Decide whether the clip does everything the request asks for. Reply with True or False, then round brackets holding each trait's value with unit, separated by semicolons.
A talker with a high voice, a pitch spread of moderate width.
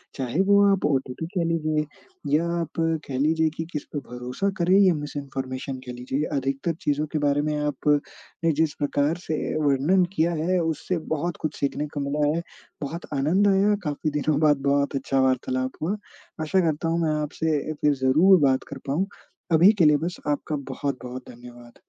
False (150 Hz; 3.2 semitones)